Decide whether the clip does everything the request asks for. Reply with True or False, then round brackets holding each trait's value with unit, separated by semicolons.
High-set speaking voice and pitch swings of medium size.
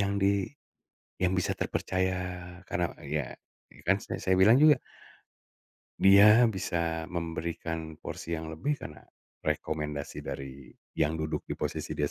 False (85 Hz; 3.6 semitones)